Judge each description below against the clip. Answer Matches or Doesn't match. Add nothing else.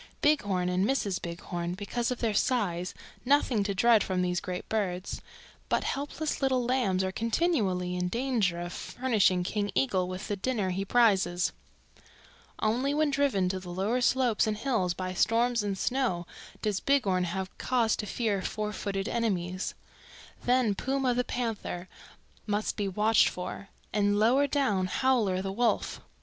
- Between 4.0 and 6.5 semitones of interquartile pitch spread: Matches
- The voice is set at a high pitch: Matches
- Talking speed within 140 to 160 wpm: Matches